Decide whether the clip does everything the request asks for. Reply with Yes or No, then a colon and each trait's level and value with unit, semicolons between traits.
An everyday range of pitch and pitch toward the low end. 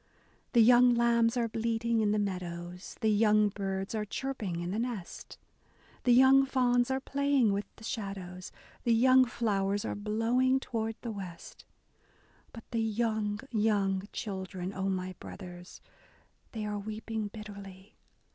No: average, 3.2 semitones; high, 215 Hz